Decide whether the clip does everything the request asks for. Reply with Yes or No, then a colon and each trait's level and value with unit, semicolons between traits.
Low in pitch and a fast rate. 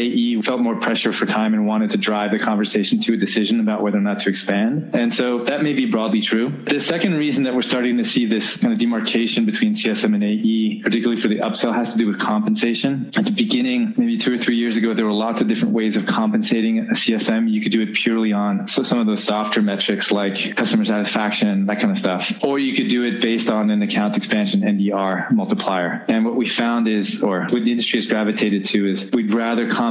Yes: low, 120 Hz; fast, 235 wpm